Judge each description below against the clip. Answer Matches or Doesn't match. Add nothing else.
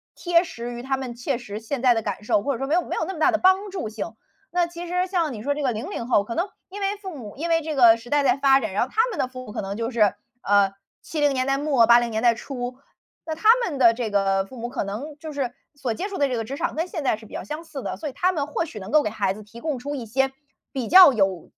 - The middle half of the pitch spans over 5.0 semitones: Matches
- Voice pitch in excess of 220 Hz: Matches